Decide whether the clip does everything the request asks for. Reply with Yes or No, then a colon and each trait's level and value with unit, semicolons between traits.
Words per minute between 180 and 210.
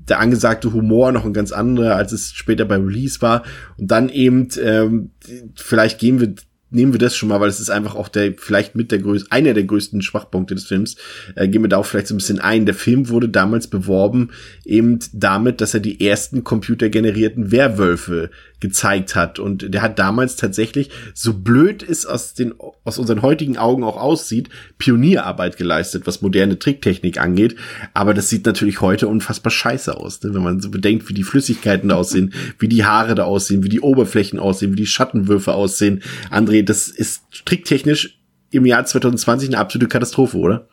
Yes: fast, 190 wpm